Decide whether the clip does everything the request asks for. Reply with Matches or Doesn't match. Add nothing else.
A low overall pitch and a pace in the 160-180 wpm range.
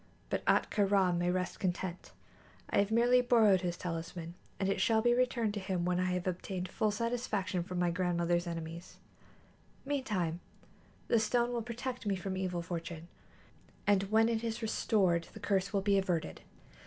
Doesn't match